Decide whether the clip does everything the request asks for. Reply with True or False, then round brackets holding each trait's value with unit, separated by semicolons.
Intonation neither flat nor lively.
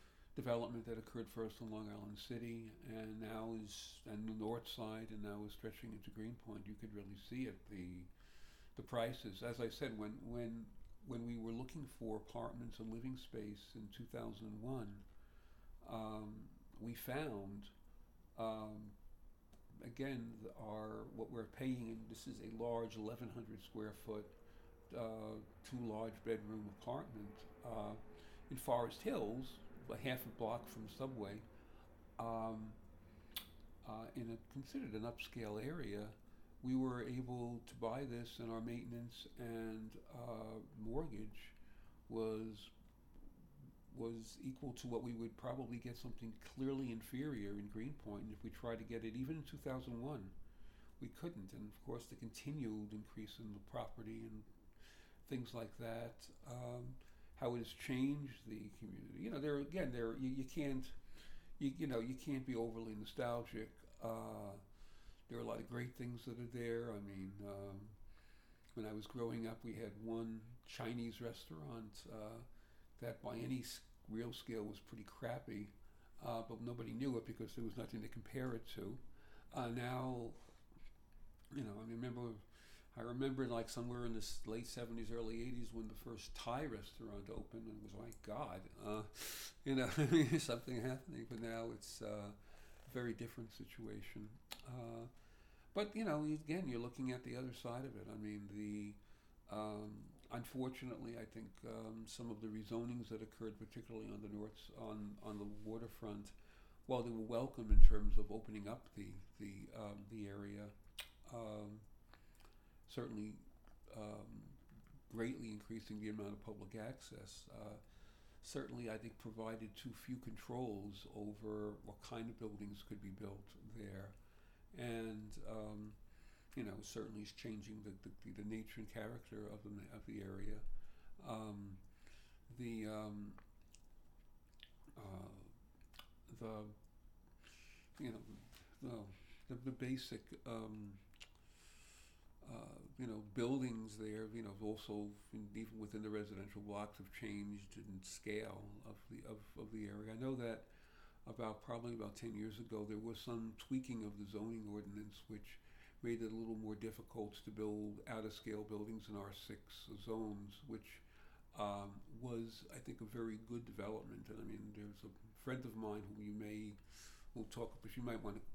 False (2.1 semitones)